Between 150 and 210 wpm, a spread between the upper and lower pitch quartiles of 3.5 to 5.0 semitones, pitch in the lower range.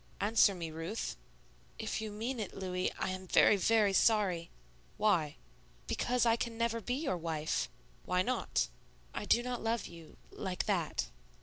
No: average, 160 wpm; average, 4.1 semitones; high, 205 Hz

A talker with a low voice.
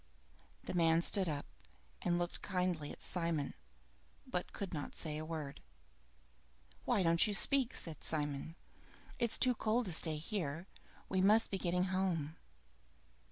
No: medium, 175 Hz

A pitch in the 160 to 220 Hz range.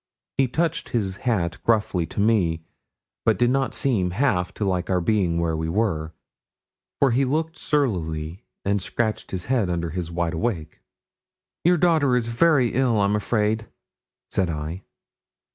No: low, 105 Hz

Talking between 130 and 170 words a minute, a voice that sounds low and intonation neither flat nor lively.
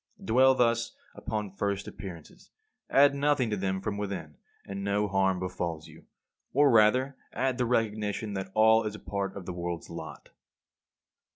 Yes: average, 155 wpm; low, 105 Hz; average, 3.3 semitones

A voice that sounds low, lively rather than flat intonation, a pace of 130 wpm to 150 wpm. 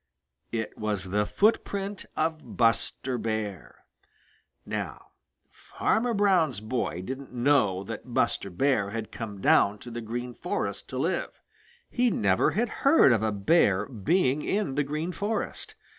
Yes: low, 120 Hz; wide, 7.5 semitones; average, 140 wpm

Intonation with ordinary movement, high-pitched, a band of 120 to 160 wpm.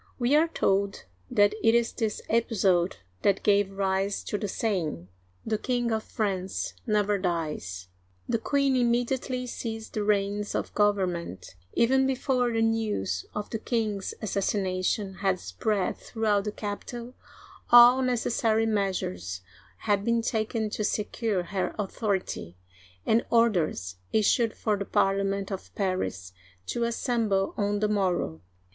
Yes: average, 3.1 semitones; high, 205 Hz; slow, 135 wpm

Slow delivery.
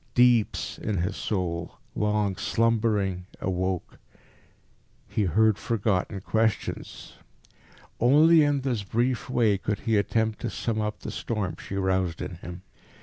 Yes: slow, 130 wpm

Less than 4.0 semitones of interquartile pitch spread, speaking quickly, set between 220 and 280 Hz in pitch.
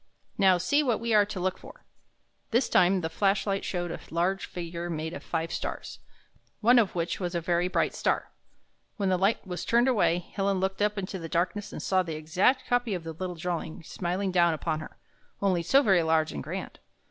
No: average, 2.9 semitones; fast, 210 wpm; medium, 185 Hz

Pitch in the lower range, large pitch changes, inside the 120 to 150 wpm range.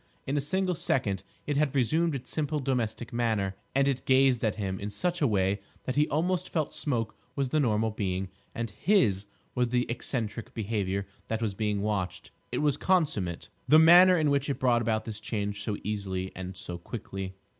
No: low, 115 Hz; wide, 5.9 semitones; average, 190 wpm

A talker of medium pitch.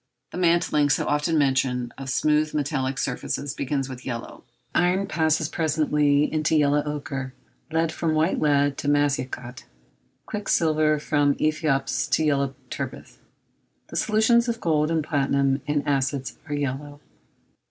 Yes: medium, 145 Hz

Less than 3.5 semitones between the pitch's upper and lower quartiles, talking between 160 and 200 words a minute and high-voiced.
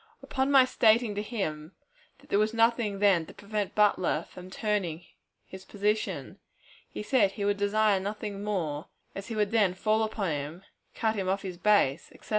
Yes: narrow, 2.5 semitones; average, 185 wpm; high, 205 Hz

